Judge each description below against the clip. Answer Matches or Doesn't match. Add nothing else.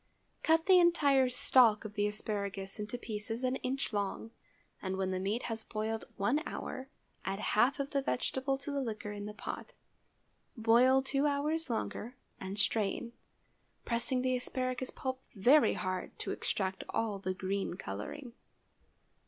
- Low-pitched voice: Doesn't match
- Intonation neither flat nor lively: Matches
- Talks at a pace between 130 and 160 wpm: Matches